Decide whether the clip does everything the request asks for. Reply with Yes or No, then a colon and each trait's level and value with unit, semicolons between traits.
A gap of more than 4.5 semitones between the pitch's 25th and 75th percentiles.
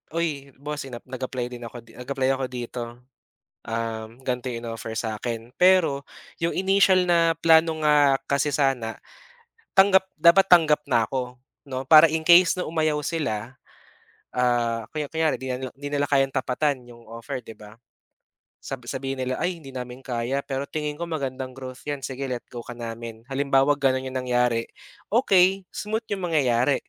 No: average, 4.2 semitones